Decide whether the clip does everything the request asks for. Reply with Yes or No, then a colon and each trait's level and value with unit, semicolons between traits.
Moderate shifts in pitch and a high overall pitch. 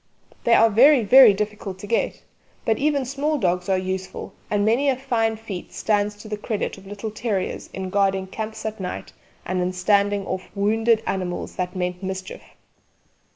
Yes: average, 3.0 semitones; high, 205 Hz